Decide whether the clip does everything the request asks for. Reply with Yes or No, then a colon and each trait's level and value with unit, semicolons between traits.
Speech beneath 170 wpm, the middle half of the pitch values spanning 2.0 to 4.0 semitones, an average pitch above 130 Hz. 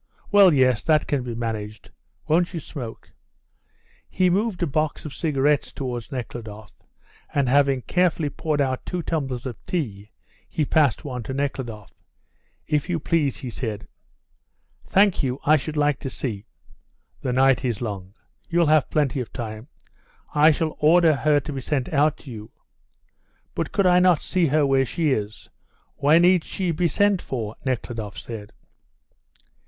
No: average, 160 wpm; average, 4.8 semitones; medium, 140 Hz